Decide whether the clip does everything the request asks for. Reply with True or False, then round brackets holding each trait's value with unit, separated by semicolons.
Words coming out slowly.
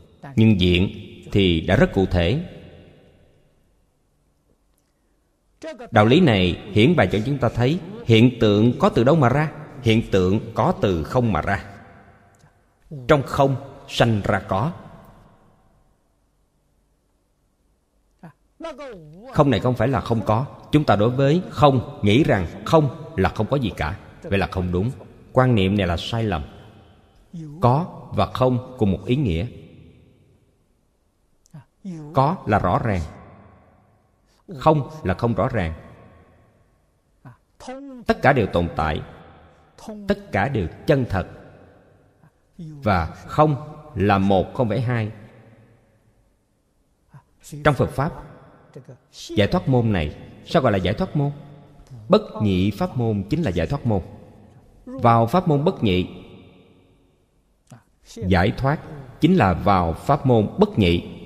True (130 wpm)